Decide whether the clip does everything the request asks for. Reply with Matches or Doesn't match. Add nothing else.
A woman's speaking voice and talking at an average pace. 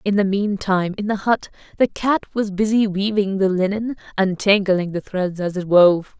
Matches